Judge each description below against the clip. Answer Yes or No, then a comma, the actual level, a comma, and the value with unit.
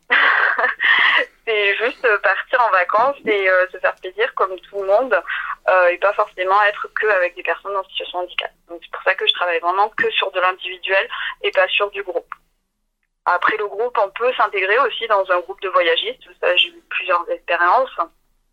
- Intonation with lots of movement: Yes, wide, 8.6 semitones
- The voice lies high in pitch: Yes, high, 200 Hz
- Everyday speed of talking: Yes, average, 190 wpm